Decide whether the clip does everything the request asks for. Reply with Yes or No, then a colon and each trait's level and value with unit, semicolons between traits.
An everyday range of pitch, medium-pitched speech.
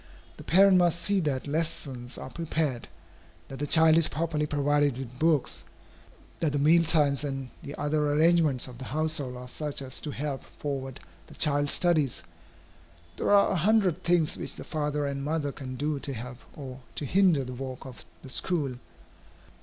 Yes: average, 3.2 semitones; medium, 145 Hz